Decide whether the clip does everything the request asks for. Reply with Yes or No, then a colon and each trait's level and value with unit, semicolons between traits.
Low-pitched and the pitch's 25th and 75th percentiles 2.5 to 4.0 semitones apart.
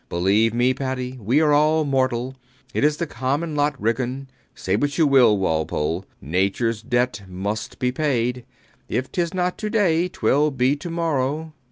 No: low, 130 Hz; average, 4.8 semitones